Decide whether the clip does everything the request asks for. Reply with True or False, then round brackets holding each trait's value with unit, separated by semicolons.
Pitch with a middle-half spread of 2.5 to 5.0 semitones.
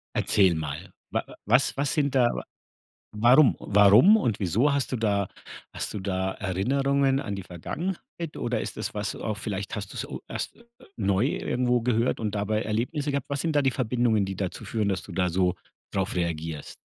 False (5.6 semitones)